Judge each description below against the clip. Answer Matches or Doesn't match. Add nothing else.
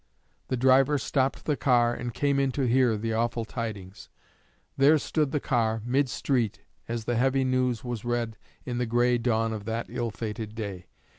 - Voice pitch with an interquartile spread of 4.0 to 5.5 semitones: Doesn't match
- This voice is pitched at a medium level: Doesn't match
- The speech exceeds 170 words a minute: Matches